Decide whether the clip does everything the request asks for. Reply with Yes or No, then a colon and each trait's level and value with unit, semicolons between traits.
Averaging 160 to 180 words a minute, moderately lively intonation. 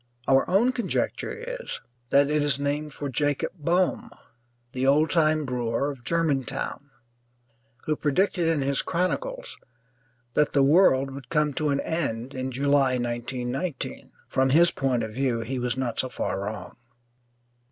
No: average, 145 wpm; average, 3.6 semitones